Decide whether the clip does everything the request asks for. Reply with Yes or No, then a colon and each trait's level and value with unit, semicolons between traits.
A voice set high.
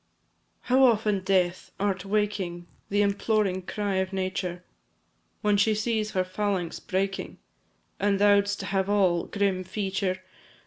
Yes: high, 195 Hz